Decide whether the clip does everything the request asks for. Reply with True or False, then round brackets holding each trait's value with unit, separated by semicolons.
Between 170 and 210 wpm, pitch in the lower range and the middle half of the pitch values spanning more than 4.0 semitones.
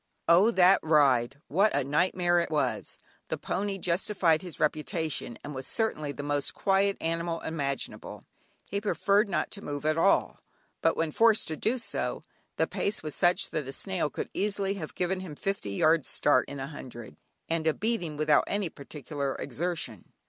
False (175 wpm; 165 Hz; 4.9 semitones)